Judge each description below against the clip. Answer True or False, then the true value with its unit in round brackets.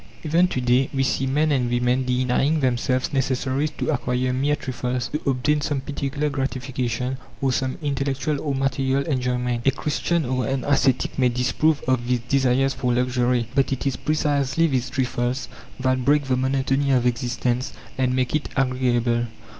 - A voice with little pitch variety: True (1.8 semitones)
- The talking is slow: False (165 wpm)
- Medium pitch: False (130 Hz)